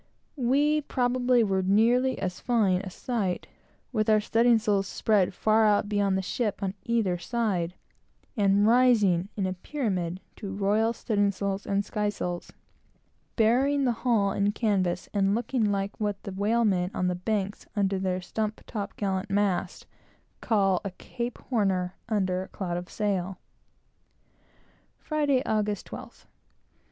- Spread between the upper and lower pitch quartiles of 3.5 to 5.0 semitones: No, average, 3.0 semitones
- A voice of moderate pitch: No, high, 205 Hz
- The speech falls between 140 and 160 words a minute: Yes, average, 145 wpm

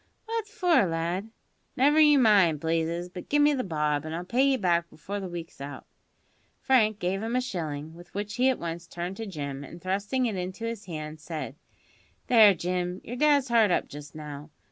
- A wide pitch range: Yes, wide, 6.2 semitones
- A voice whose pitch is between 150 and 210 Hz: Yes, medium, 185 Hz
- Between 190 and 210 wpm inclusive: Yes, average, 200 wpm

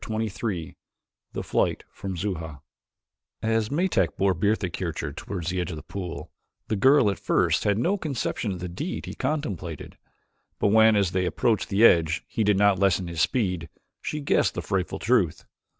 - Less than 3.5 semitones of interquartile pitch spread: No, average, 4.2 semitones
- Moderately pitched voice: No, low, 100 Hz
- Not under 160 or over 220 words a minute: Yes, average, 180 wpm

